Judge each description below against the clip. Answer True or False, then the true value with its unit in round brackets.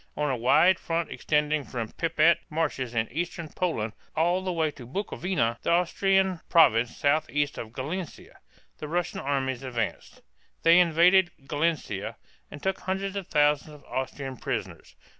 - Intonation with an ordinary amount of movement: True (4.5 semitones)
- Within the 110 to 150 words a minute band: False (160 wpm)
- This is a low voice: False (155 Hz)